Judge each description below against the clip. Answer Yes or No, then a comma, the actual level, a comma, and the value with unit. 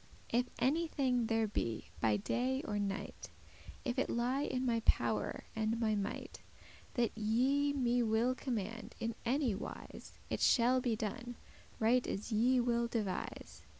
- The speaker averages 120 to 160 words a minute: Yes, average, 150 wpm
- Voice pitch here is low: No, high, 235 Hz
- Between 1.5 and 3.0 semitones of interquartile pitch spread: Yes, narrow, 2.6 semitones